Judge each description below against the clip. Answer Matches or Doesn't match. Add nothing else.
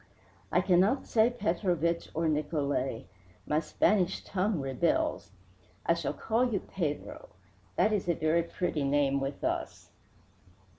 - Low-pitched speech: Doesn't match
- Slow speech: Matches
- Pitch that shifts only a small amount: Doesn't match